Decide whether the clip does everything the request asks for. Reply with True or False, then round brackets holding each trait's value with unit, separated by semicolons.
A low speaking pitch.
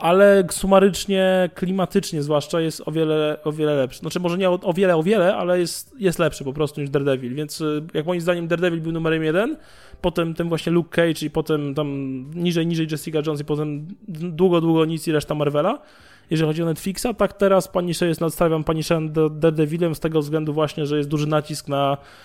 False (160 Hz)